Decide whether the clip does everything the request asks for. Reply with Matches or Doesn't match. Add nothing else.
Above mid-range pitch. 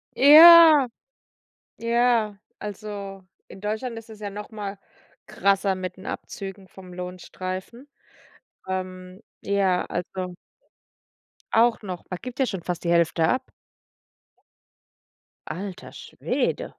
Matches